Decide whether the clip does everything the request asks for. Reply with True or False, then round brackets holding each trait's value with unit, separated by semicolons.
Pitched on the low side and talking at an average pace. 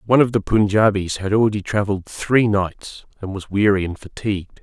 True (100 Hz; 180 wpm)